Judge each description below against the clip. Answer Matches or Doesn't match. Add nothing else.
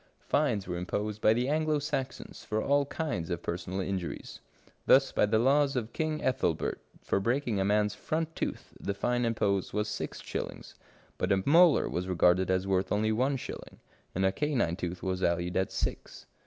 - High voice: Doesn't match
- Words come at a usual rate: Matches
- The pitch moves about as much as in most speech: Doesn't match